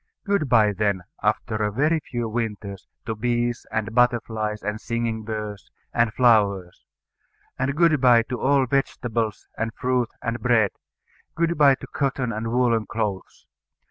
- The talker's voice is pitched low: Yes, low, 115 Hz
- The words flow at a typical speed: Yes, average, 145 wpm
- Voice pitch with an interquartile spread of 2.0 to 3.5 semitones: Yes, average, 2.8 semitones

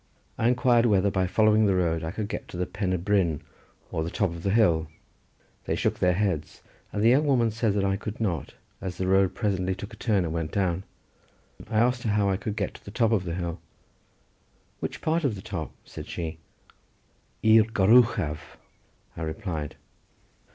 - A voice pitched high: No, low, 100 Hz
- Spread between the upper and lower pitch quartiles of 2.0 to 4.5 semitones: Yes, average, 3.9 semitones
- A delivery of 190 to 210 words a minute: Yes, average, 200 wpm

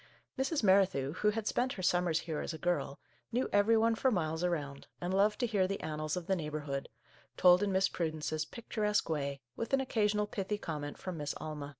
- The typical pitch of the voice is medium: Yes, medium, 180 Hz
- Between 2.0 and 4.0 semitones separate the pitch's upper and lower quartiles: No, average, 5.2 semitones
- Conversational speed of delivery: No, fast, 220 wpm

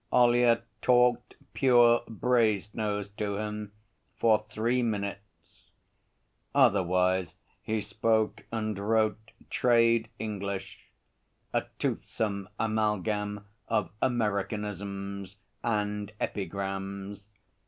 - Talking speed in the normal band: No, slow, 80 wpm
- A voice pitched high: No, low, 105 Hz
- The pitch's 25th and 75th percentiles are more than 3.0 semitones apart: No, narrow, 2.4 semitones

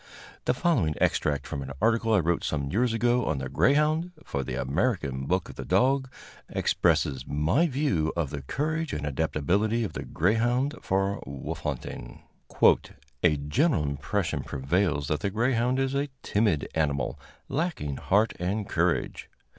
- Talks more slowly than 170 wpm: Yes, average, 155 wpm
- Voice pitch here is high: No, very low, 95 Hz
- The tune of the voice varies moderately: No, wide, 9.0 semitones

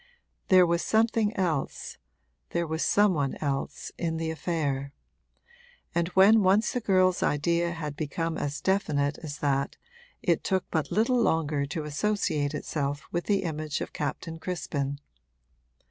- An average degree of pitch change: Yes, average, 4.2 semitones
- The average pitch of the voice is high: No, medium, 165 Hz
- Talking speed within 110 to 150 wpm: Yes, average, 145 wpm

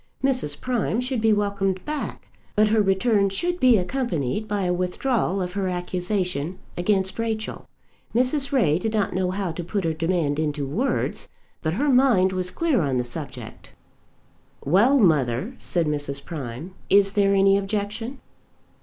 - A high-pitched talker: Yes, high, 195 Hz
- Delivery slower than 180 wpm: Yes, average, 155 wpm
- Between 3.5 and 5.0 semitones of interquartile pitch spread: Yes, average, 4.3 semitones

